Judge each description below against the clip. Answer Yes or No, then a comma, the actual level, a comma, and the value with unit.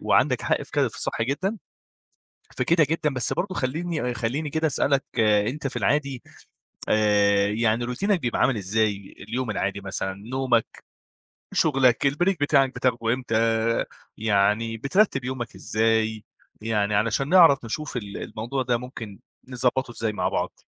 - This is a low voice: Yes, low, 120 Hz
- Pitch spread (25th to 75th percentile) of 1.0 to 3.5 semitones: No, average, 4.2 semitones